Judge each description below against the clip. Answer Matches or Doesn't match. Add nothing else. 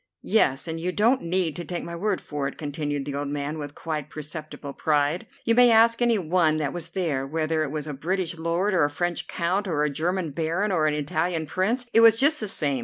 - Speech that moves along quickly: Matches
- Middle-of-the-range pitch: Matches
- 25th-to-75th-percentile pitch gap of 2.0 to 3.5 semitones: Doesn't match